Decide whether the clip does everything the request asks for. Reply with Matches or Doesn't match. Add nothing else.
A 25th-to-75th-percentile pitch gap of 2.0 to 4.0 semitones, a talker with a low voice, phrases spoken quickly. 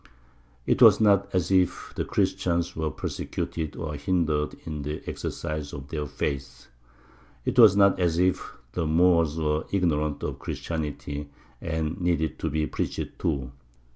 Doesn't match